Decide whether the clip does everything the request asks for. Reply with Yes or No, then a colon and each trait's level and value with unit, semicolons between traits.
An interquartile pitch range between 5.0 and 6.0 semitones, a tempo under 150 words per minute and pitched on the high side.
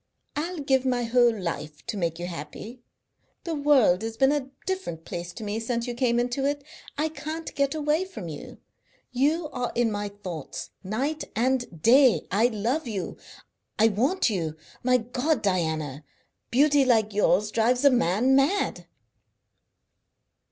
No: wide, 5.4 semitones; average, 155 wpm; high, 240 Hz